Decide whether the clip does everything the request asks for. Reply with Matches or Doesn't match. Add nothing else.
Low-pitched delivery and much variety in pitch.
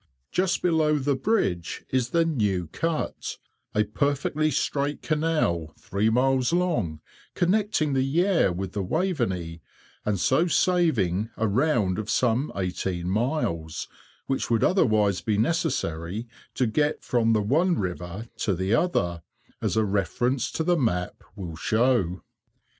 Matches